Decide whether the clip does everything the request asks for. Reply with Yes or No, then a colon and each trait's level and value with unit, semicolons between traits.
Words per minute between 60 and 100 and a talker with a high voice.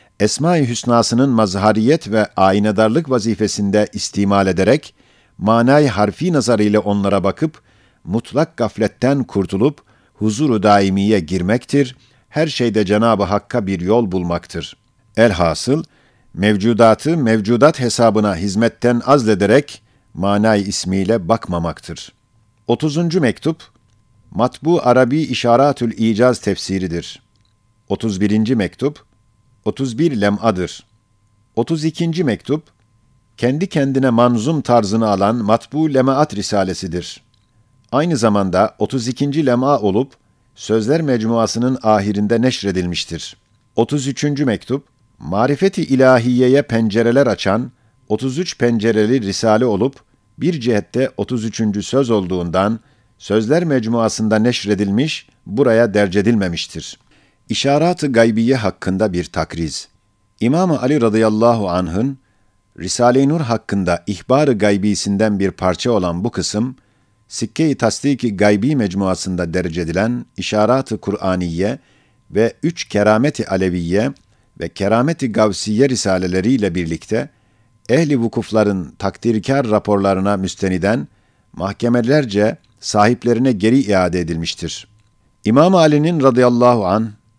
No: slow, 95 wpm; low, 115 Hz